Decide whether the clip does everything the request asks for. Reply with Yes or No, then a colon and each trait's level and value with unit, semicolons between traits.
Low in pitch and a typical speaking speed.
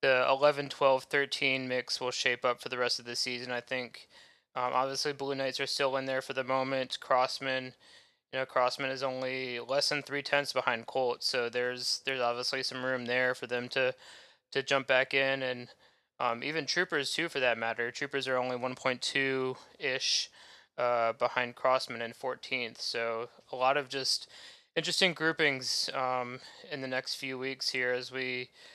Yes: low, 130 Hz; average, 180 wpm